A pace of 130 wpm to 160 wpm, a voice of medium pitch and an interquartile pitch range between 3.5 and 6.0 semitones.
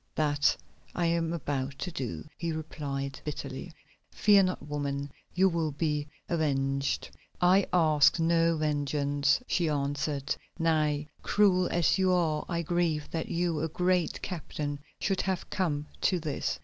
No: average, 140 wpm; medium, 155 Hz; average, 3.1 semitones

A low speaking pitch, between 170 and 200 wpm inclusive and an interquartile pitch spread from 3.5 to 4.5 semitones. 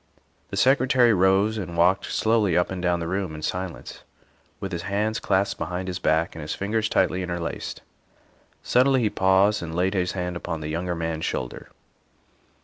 No: very low, 95 Hz; average, 175 wpm; average, 2.8 semitones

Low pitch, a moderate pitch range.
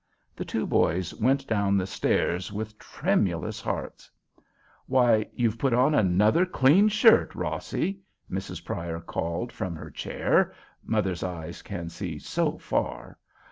No: low, 105 Hz; wide, 6.7 semitones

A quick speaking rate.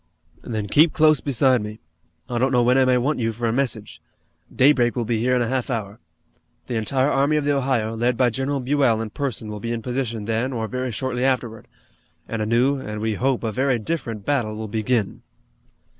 Yes: fast, 215 wpm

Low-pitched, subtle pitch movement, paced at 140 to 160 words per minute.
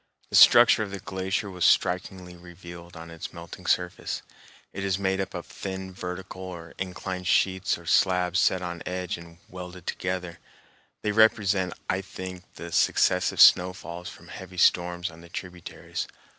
Yes: very low, 90 Hz; narrow, 1.4 semitones; average, 155 wpm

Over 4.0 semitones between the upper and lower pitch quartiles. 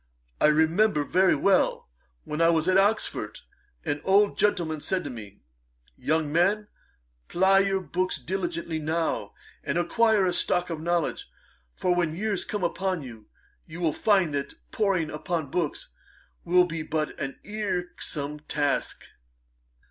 No: average, 3.6 semitones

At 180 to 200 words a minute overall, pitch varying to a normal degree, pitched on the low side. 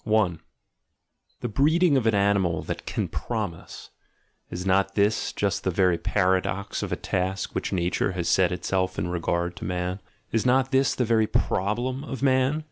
No: average, 170 wpm; average, 5.0 semitones; low, 100 Hz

